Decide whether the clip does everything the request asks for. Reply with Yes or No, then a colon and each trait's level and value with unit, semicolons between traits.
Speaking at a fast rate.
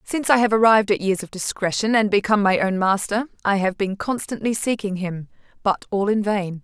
Yes: fast, 210 wpm